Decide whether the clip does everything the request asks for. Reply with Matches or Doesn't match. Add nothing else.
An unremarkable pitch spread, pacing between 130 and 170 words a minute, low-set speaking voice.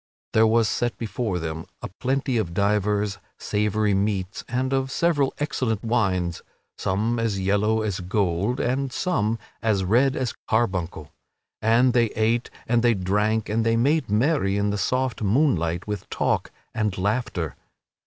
Matches